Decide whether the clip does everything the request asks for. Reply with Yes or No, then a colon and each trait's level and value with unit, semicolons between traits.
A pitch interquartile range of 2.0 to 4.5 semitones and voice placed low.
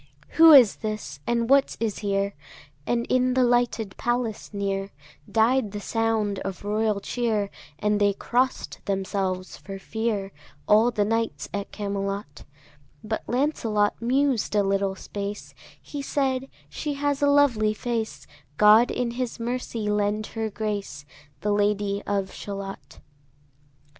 No: average, 3.2 semitones; high, 215 Hz